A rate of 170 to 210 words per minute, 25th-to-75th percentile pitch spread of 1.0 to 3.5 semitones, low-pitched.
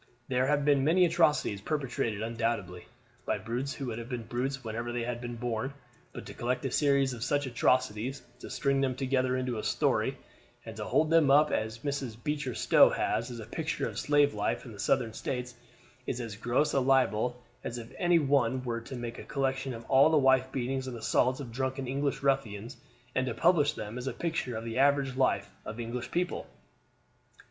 Yes: fast, 205 wpm; average, 2.9 semitones; low, 130 Hz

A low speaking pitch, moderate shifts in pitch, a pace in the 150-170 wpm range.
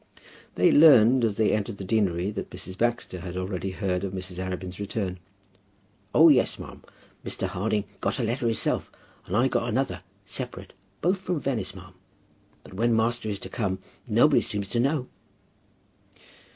Yes: low, 105 Hz; average, 4.3 semitones; average, 165 wpm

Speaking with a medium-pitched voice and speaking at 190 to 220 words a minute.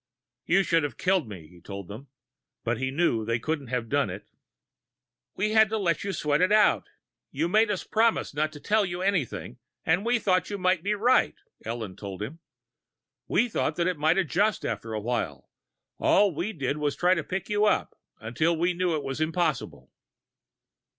Yes: medium, 165 Hz; average, 195 wpm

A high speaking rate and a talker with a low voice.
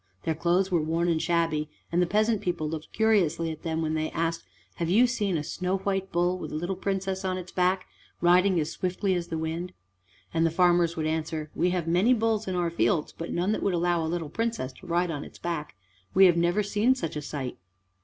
No: fast, 230 wpm; medium, 175 Hz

